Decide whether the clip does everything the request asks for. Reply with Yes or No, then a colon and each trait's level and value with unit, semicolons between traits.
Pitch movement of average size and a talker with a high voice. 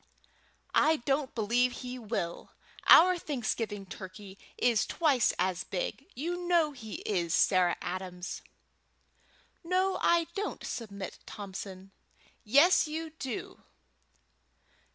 No: wide, 8.1 semitones; high, 235 Hz